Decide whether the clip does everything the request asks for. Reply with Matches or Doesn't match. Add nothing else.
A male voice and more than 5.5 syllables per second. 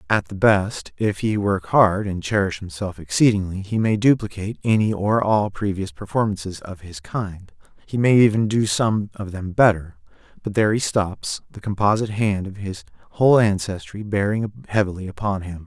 Doesn't match